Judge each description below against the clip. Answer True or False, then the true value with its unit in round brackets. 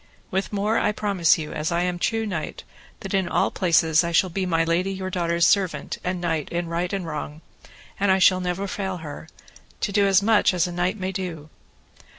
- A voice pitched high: False (180 Hz)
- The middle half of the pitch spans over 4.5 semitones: False (2.5 semitones)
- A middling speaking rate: False (215 wpm)